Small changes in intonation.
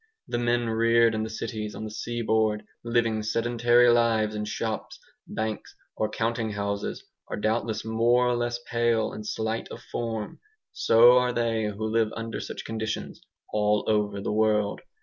Yes: narrow, 1.5 semitones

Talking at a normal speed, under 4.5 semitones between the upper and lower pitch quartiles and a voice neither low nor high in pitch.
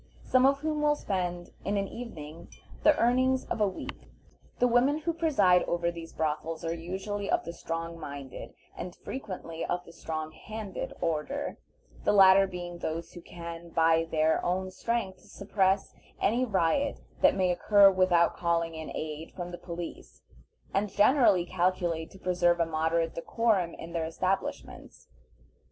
Yes: average, 155 wpm; average, 3.6 semitones; medium, 180 Hz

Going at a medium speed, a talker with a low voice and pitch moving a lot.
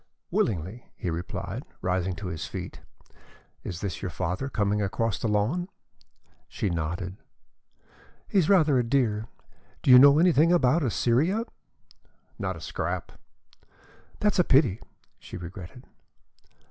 No: slow, 125 wpm; low, 110 Hz; wide, 7.4 semitones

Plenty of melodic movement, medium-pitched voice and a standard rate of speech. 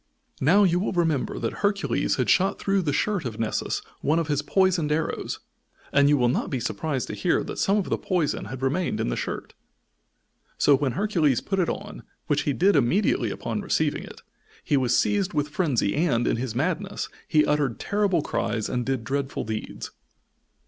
Yes: wide, 5.9 semitones; medium, 150 Hz; average, 190 wpm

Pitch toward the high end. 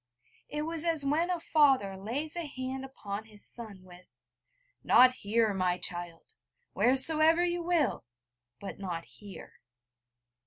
Yes: very high, 255 Hz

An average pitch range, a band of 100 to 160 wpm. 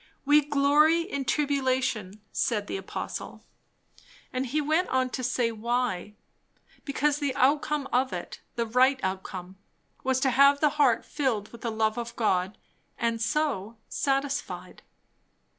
Yes: average, 3.8 semitones; average, 140 wpm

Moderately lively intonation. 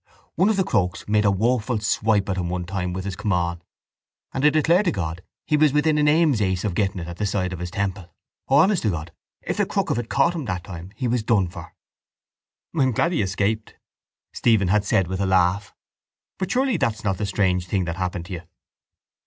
No: wide, 6.2 semitones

